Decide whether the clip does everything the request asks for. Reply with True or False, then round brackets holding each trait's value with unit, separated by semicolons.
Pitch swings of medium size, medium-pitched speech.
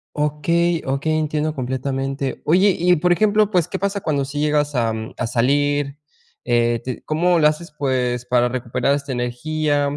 True (3.7 semitones; 145 Hz)